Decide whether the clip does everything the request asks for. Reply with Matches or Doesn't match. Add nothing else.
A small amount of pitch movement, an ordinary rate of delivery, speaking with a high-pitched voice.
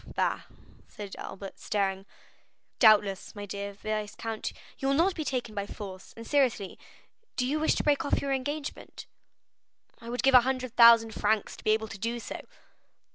Doesn't match